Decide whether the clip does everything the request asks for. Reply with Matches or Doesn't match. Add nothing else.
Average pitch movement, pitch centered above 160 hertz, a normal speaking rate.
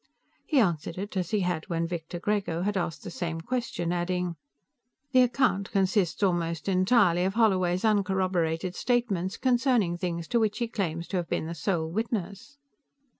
Matches